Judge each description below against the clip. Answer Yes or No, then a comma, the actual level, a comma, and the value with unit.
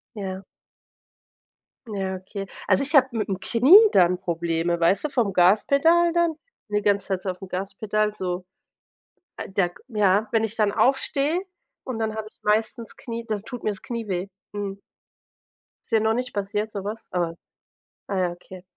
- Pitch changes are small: No, average, 3.2 semitones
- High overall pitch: Yes, high, 205 Hz